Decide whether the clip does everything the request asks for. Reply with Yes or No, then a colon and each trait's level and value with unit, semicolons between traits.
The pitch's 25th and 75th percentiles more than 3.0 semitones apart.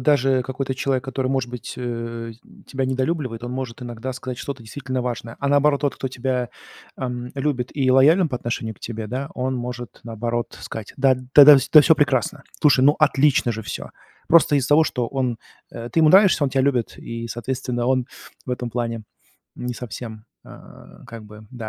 No: narrow, 2.5 semitones